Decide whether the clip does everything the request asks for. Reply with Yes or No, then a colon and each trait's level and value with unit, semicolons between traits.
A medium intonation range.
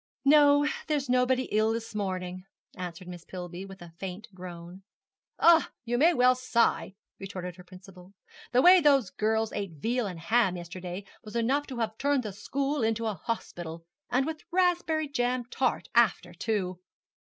No: wide, 6.0 semitones